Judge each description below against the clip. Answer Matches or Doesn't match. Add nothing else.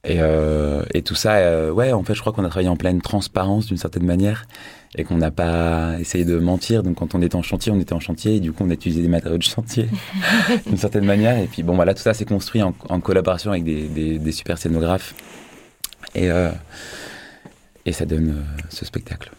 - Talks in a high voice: Doesn't match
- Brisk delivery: Matches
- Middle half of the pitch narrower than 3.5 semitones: Doesn't match